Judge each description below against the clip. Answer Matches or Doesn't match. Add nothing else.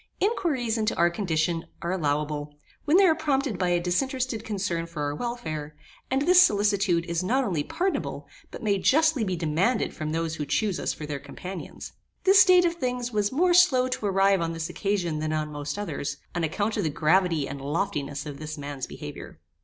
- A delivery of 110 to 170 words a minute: Doesn't match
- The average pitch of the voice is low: Doesn't match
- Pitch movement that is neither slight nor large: Doesn't match